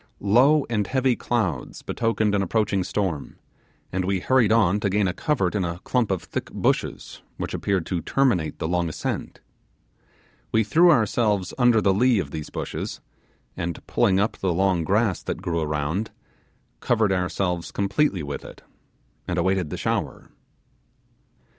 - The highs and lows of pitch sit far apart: No, average, 4.3 semitones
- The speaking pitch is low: Yes, low, 100 Hz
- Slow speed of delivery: No, average, 155 wpm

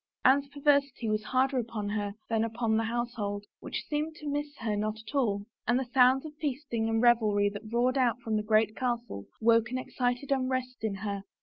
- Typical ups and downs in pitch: Yes, average, 3.3 semitones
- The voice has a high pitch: Yes, high, 235 Hz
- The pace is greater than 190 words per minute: Yes, average, 200 wpm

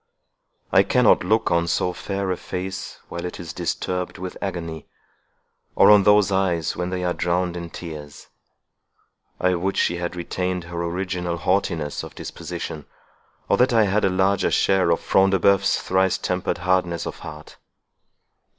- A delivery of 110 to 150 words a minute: No, average, 160 wpm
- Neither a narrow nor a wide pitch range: No, narrow, 1.9 semitones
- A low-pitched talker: Yes, very low, 90 Hz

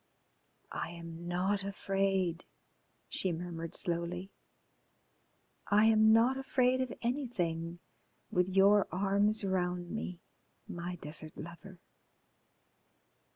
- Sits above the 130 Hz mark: Yes, medium, 185 Hz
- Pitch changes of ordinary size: Yes, average, 3.1 semitones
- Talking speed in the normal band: No, slow, 95 wpm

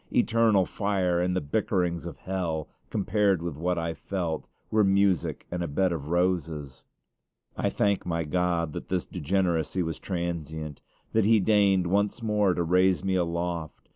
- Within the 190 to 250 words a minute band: No, average, 160 wpm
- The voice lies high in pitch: No, very low, 90 Hz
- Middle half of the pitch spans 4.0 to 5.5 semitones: No, average, 2.7 semitones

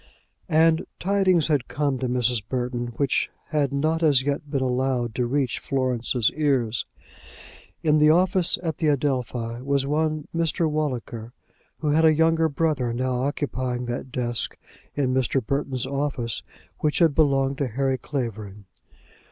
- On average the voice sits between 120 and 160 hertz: Yes, low, 135 Hz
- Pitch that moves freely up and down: No, average, 3.6 semitones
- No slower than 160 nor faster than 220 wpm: No, average, 145 wpm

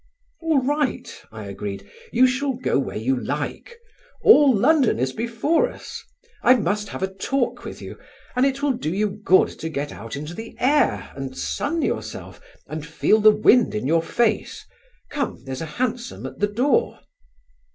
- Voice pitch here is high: Yes, high, 220 Hz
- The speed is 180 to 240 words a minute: No, average, 170 wpm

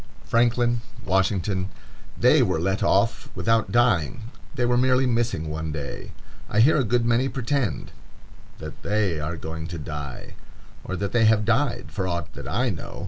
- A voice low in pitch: Yes, low, 110 Hz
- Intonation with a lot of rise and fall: Yes, wide, 5.7 semitones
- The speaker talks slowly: No, average, 155 wpm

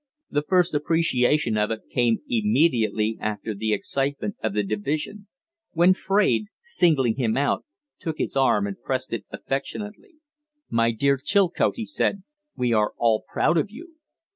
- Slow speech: No, average, 150 wpm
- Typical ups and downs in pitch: No, wide, 8.5 semitones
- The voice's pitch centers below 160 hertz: Yes, medium, 140 Hz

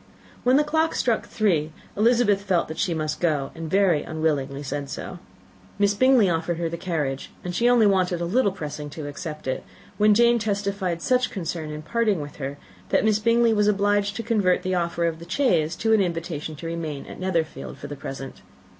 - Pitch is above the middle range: No, medium, 180 Hz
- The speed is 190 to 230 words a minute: Yes, average, 200 wpm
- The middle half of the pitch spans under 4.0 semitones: No, average, 5.0 semitones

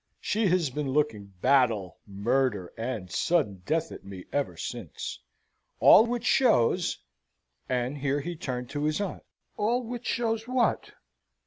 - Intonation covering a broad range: Yes, wide, 8.8 semitones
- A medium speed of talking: Yes, average, 145 wpm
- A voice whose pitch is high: No, medium, 140 Hz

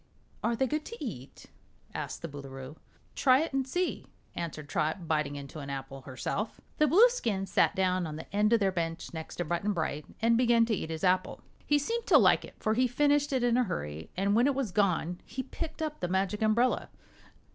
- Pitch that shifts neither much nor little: No, wide, 8.1 semitones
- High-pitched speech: Yes, high, 200 Hz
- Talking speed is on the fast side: Yes, fast, 210 wpm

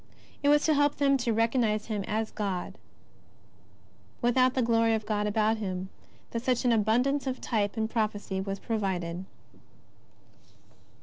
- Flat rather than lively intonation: No, average, 3.1 semitones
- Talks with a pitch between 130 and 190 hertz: No, high, 225 Hz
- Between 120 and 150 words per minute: Yes, average, 145 wpm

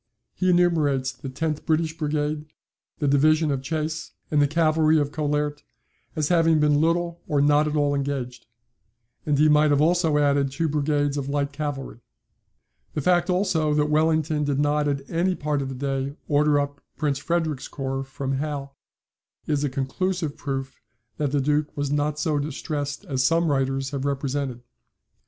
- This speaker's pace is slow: No, average, 170 wpm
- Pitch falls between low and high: Yes, medium, 145 Hz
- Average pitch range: No, narrow, 1.8 semitones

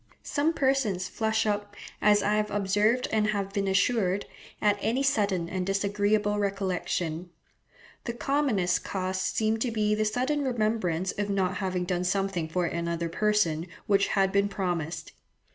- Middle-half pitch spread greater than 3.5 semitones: No, average, 2.7 semitones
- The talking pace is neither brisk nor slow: Yes, average, 150 wpm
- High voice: Yes, high, 200 Hz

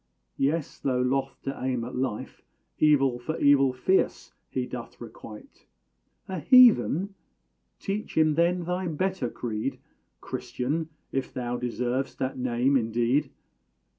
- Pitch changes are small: No, average, 4.3 semitones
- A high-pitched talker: No, low, 135 Hz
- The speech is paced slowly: Yes, slow, 125 wpm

